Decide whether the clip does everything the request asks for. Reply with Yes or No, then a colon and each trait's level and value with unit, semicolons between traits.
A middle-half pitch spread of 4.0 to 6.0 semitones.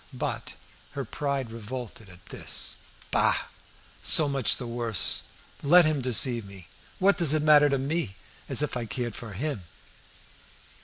Yes: average, 4.6 semitones